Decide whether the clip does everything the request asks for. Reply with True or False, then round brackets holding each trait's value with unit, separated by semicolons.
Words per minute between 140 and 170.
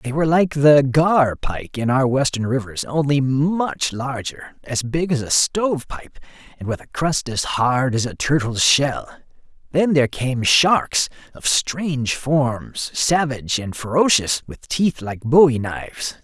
True (155 wpm)